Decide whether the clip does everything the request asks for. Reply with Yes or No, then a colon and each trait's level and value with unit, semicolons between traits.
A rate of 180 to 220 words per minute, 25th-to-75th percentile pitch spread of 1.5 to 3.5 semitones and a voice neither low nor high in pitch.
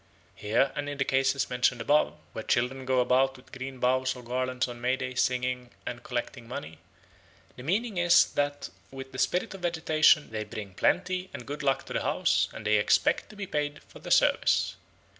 No: average, 195 wpm; average, 2.8 semitones; low, 130 Hz